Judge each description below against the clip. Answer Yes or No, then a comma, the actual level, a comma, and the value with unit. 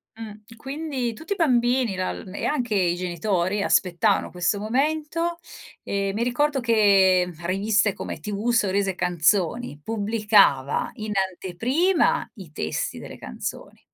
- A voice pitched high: Yes, high, 210 Hz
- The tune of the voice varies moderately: Yes, average, 4.7 semitones